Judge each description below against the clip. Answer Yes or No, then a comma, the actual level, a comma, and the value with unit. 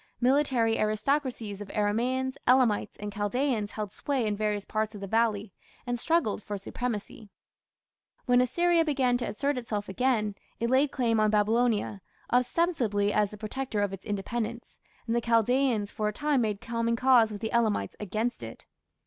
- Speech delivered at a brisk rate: No, average, 165 wpm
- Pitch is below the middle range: No, high, 230 Hz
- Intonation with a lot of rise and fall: No, average, 3.3 semitones